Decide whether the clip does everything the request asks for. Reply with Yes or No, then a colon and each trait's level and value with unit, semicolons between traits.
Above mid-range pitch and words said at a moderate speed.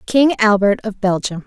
Yes: high, 210 Hz; average, 165 wpm